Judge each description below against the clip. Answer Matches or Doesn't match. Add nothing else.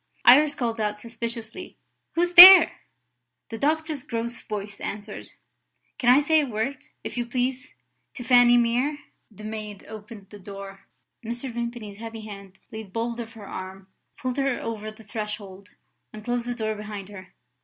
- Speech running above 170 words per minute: Doesn't match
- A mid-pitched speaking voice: Doesn't match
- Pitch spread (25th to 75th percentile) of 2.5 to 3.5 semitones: Matches